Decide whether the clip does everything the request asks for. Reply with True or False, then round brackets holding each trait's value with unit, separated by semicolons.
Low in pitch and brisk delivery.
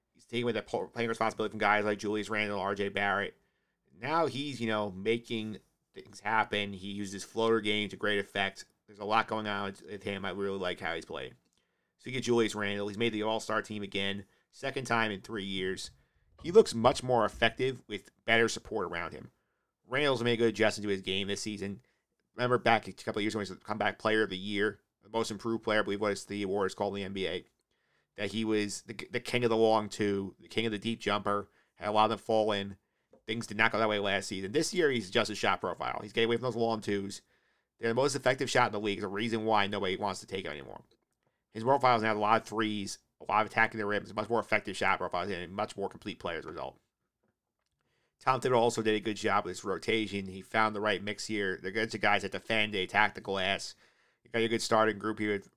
True (105 Hz; 250 wpm)